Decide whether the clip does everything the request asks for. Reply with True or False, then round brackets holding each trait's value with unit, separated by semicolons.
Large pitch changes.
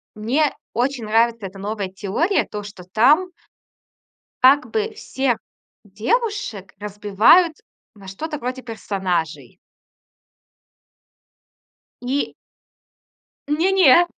True (6.9 semitones)